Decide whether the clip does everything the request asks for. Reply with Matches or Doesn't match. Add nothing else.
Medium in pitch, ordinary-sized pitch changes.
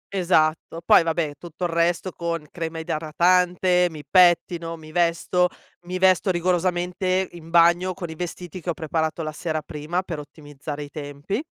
Doesn't match